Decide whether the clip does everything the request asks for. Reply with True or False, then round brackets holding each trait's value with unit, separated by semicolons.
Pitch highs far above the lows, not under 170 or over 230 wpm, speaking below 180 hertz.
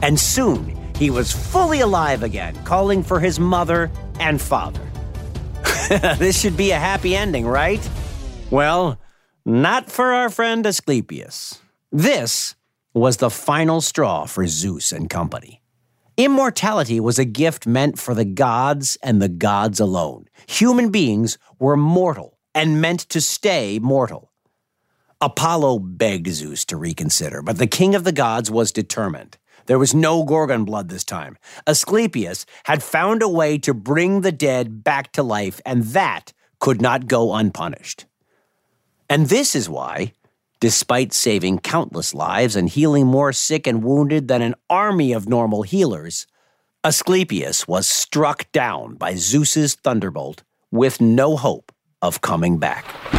False (6.5 semitones; 145 wpm; 140 Hz)